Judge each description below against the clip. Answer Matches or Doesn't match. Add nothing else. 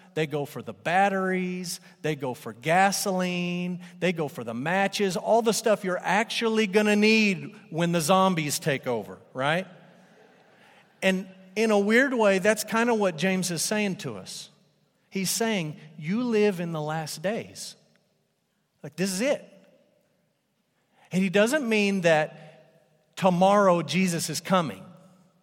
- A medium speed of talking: Matches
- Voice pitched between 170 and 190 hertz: Matches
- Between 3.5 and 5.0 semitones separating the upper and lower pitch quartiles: Matches